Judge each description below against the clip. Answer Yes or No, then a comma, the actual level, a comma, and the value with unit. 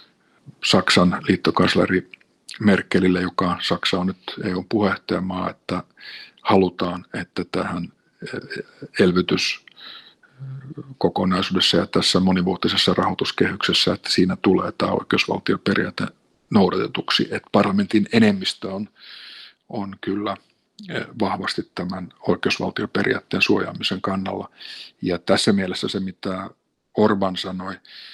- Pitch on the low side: Yes, very low, 95 Hz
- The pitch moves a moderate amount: No, narrow, 2.3 semitones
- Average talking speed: No, slow, 90 wpm